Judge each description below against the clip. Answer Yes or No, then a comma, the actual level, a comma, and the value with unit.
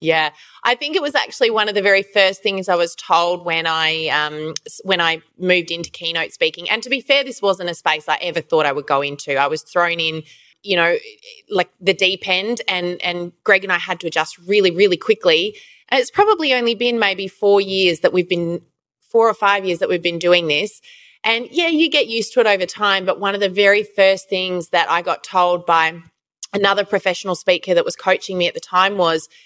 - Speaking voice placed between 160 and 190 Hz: Yes, medium, 185 Hz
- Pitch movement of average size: Yes, average, 3.8 semitones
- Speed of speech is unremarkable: No, fast, 230 wpm